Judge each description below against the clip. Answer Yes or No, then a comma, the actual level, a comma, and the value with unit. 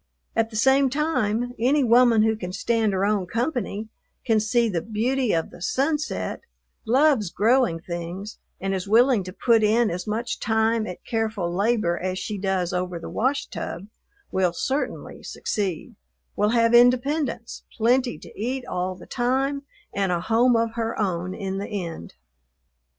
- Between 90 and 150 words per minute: No, average, 160 wpm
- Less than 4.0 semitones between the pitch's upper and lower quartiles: No, average, 4.3 semitones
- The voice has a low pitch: No, high, 220 Hz